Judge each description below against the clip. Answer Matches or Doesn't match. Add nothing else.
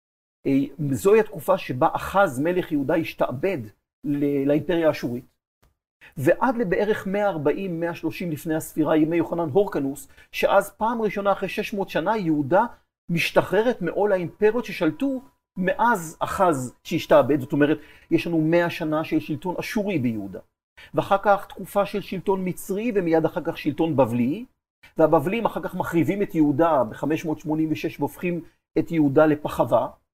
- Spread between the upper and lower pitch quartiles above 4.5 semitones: Doesn't match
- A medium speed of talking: Matches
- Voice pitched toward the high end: Doesn't match